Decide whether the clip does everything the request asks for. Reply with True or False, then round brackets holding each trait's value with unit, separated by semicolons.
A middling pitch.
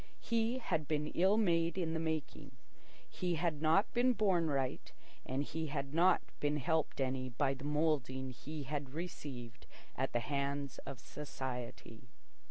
True (150 Hz)